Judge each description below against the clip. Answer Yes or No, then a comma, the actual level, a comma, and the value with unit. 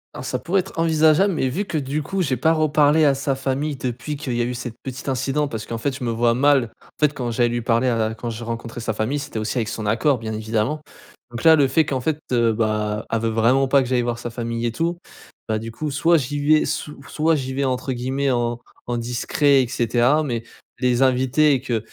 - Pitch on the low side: Yes, low, 130 Hz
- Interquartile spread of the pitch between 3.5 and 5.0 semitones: Yes, average, 3.8 semitones